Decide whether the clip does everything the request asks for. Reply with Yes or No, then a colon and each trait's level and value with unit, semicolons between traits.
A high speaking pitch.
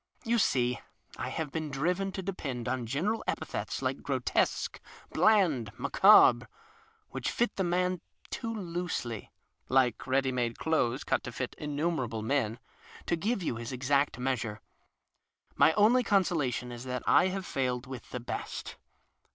No: medium, 140 Hz